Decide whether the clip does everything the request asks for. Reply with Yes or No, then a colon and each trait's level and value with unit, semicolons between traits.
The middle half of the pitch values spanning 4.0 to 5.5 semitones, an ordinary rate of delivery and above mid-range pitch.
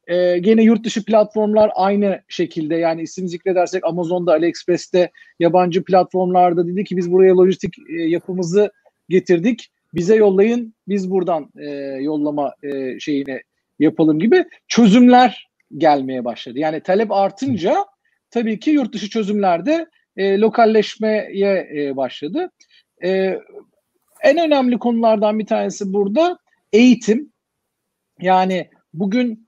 Yes: average, 4.4 semitones; average, 110 wpm; high, 195 Hz